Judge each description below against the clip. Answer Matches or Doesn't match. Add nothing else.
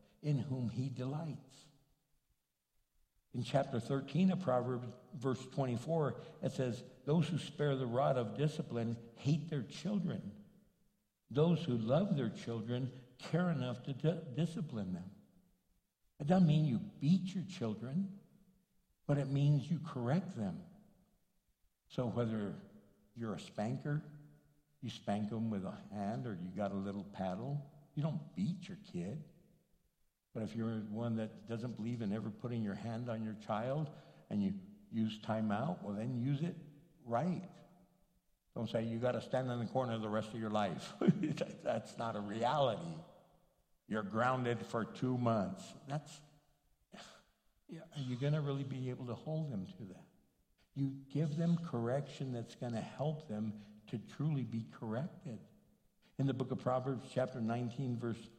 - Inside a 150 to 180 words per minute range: Matches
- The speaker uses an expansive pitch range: Matches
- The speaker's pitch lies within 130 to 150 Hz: Matches